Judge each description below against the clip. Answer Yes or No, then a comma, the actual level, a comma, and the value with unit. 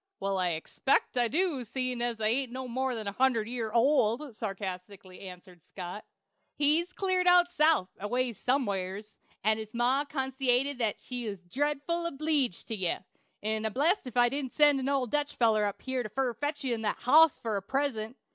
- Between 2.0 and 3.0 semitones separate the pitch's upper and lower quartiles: No, average, 4.7 semitones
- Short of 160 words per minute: No, average, 175 wpm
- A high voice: Yes, high, 245 Hz